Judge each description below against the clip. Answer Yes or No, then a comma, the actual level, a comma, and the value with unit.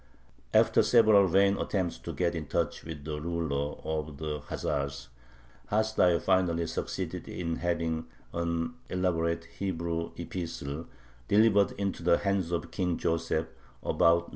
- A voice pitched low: Yes, very low, 85 Hz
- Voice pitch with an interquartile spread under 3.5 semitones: Yes, narrow, 2.4 semitones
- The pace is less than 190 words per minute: Yes, slow, 135 wpm